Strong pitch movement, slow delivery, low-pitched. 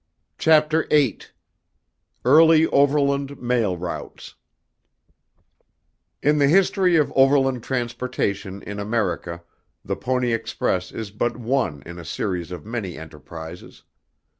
Yes: wide, 7.3 semitones; slow, 110 wpm; low, 120 Hz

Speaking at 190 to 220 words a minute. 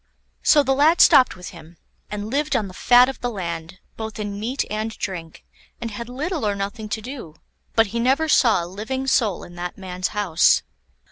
Yes: average, 200 wpm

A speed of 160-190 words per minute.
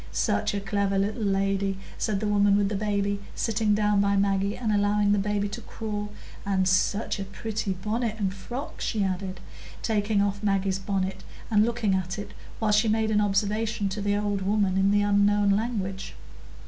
Yes: average, 180 wpm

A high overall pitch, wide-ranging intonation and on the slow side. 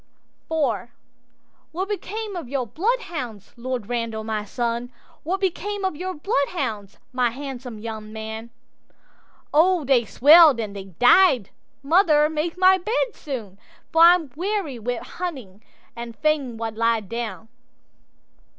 Yes: very high, 260 Hz; wide, 7.1 semitones; slow, 115 wpm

